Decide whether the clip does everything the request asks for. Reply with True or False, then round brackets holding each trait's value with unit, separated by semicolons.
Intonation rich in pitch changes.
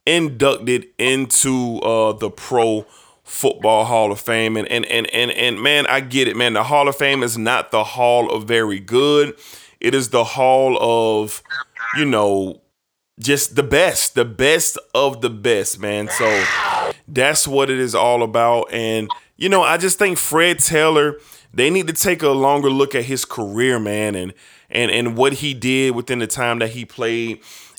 False (3.9 semitones)